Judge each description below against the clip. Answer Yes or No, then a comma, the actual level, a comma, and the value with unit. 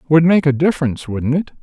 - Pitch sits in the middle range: Yes, medium, 150 Hz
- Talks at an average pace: No, fast, 220 wpm